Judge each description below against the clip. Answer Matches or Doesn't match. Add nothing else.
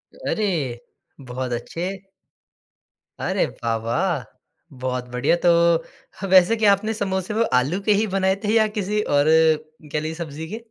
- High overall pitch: Doesn't match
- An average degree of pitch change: Doesn't match